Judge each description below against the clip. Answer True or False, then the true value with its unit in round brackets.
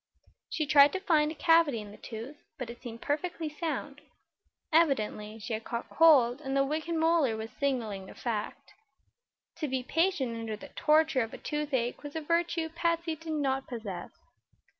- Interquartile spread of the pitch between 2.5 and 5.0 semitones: False (5.4 semitones)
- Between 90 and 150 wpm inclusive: False (175 wpm)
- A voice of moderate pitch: False (285 Hz)